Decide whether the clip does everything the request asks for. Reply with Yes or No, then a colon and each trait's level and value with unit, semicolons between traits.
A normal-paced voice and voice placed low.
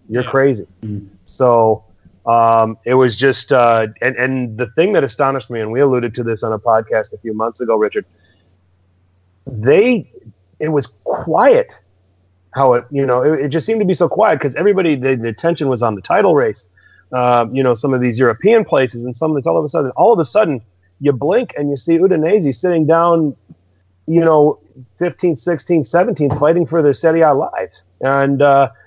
Yes: average, 195 wpm; low, 130 Hz